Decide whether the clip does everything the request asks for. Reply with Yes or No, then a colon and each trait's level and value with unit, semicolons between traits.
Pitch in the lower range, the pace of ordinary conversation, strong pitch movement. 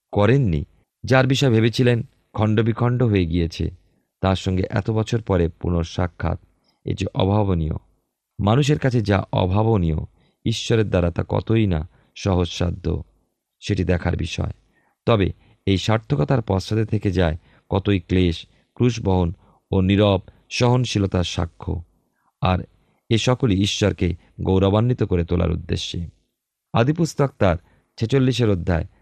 No: low, 100 Hz; average, 110 wpm; average, 4.2 semitones